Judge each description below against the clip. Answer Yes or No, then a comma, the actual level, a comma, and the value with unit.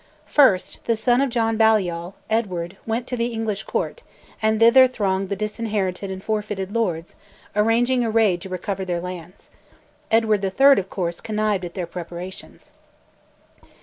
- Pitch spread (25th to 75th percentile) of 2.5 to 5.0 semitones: Yes, average, 3.5 semitones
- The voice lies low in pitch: No, high, 210 Hz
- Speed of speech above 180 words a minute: No, average, 150 wpm